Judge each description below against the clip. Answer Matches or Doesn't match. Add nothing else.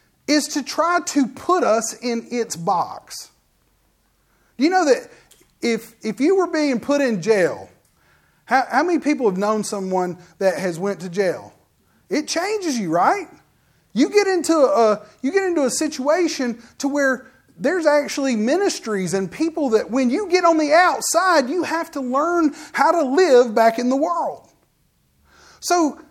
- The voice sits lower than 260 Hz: Doesn't match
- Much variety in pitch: Matches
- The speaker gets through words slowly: Doesn't match